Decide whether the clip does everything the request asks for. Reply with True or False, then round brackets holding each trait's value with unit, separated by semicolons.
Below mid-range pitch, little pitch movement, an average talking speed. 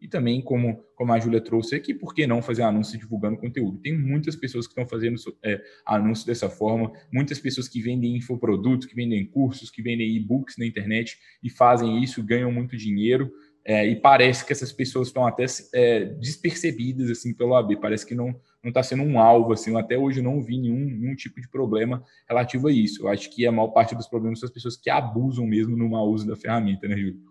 False (120 Hz; 2.2 semitones; 215 wpm)